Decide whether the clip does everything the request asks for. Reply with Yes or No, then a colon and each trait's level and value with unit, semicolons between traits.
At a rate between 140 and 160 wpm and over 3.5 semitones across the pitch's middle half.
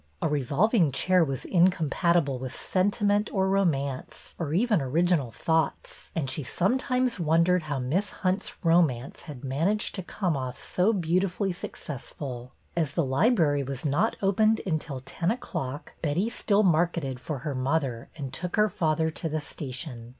Yes: average, 150 wpm; average, 5.3 semitones